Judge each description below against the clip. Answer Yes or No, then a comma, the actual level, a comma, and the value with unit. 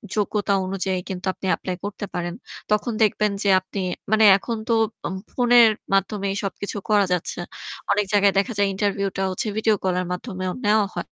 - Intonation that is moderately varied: No, narrow, 1.9 semitones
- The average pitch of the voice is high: Yes, high, 200 Hz